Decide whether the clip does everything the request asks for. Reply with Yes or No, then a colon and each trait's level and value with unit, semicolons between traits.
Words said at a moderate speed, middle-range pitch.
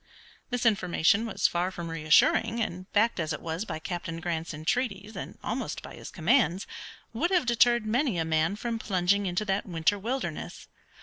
No: average, 175 wpm; high, 195 Hz